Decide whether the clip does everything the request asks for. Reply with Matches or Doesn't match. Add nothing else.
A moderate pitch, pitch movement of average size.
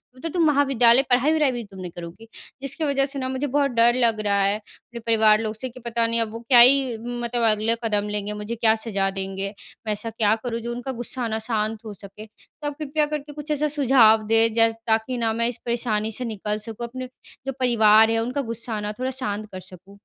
Doesn't match